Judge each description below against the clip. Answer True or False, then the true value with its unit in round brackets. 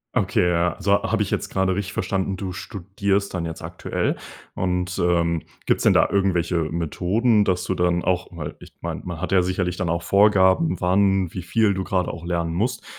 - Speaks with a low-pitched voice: True (90 Hz)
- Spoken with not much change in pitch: True (2.1 semitones)